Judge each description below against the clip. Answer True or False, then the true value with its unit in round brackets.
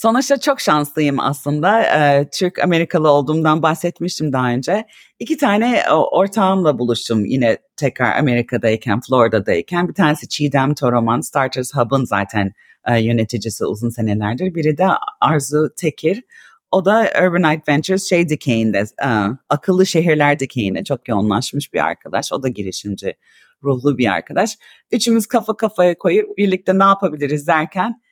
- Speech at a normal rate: True (125 wpm)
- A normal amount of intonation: False (7.2 semitones)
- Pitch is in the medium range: True (150 Hz)